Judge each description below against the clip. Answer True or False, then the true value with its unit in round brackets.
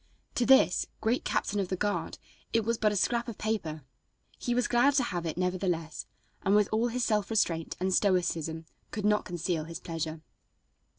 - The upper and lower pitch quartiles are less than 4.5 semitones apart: False (4.9 semitones)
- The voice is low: False (200 Hz)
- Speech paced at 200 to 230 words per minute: False (185 wpm)